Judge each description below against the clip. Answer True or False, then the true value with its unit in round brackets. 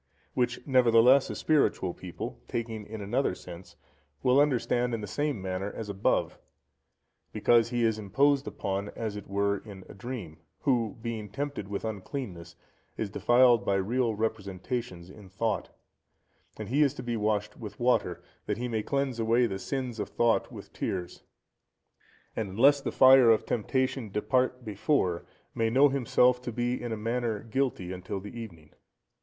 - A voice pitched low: True (115 Hz)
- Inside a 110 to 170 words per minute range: True (160 wpm)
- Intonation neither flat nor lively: True (3.8 semitones)